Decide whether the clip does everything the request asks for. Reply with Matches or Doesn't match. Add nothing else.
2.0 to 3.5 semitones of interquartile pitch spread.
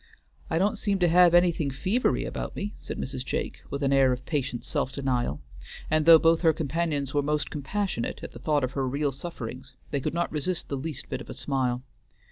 Doesn't match